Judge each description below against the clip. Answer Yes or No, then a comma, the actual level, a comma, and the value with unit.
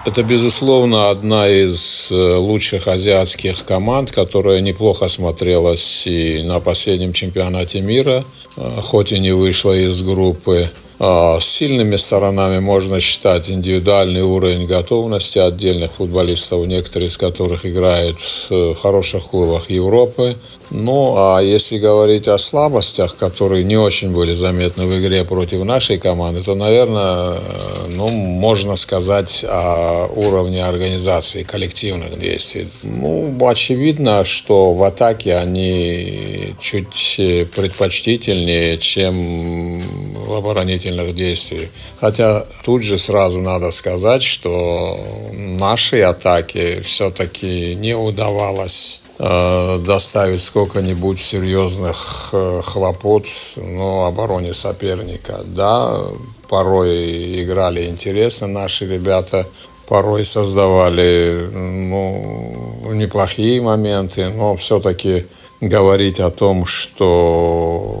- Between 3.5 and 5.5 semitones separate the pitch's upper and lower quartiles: No, narrow, 2.5 semitones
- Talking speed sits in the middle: No, slow, 100 wpm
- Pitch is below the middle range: Yes, very low, 95 Hz